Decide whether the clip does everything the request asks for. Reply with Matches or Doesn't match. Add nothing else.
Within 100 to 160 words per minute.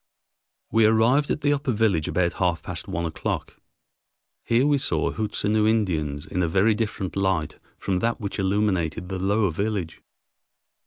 Matches